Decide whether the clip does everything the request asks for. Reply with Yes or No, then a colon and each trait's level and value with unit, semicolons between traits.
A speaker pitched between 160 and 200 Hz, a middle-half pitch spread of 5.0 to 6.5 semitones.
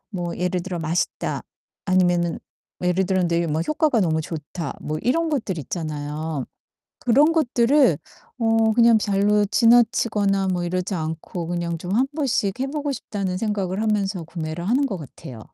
Yes: high, 190 Hz; average, 5.3 semitones